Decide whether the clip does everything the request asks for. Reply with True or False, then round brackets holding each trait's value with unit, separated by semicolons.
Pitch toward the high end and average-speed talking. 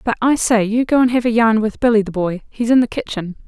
False (225 Hz; 275 wpm)